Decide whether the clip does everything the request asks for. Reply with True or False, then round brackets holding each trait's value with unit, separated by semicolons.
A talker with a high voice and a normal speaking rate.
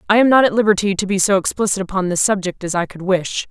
False (195 Hz; 275 wpm)